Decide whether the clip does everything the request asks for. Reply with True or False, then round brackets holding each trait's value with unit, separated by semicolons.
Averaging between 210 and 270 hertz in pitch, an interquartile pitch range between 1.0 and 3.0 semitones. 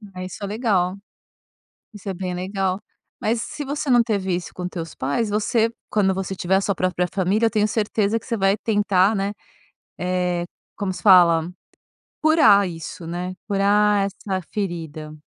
False (195 Hz; 2.6 semitones)